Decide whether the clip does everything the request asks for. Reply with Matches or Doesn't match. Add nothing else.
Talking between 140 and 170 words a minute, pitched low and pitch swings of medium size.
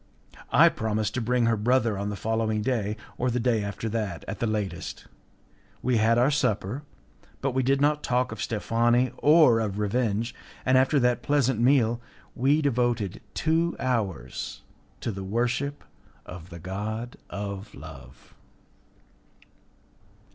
Matches